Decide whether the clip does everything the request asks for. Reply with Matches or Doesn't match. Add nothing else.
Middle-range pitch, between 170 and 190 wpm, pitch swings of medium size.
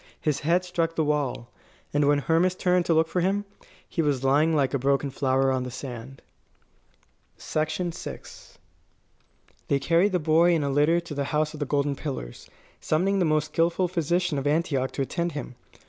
Matches